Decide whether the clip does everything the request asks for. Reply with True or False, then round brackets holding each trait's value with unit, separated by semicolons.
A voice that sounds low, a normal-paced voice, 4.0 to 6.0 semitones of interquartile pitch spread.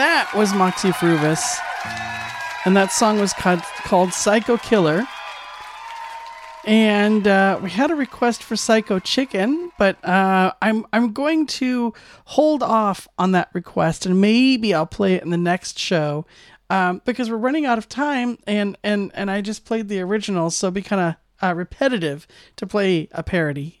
False (205 Hz; 170 wpm; 4.5 semitones)